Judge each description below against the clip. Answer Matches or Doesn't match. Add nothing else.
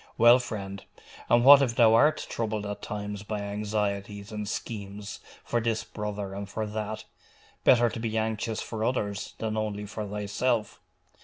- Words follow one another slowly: Doesn't match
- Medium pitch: Doesn't match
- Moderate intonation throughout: Doesn't match